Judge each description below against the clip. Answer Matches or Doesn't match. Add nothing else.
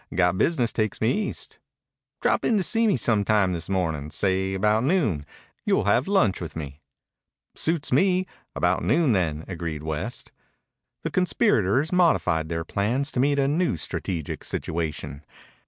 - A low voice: Matches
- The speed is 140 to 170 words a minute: Matches